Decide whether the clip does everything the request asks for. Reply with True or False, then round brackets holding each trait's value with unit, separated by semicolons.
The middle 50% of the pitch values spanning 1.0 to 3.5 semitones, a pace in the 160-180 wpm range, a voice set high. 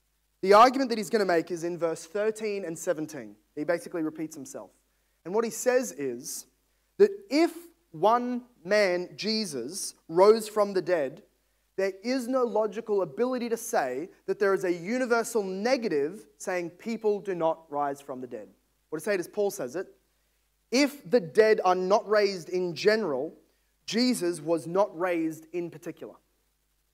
False (5.1 semitones; 165 wpm; 200 Hz)